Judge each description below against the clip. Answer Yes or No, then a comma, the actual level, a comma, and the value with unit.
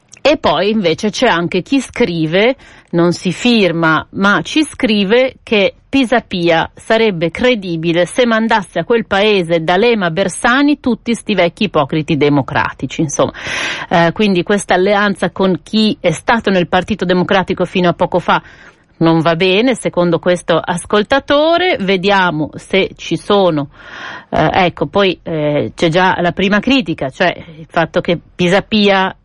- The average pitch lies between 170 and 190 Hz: Yes, medium, 185 Hz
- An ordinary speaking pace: Yes, average, 145 wpm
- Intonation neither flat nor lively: Yes, average, 4.1 semitones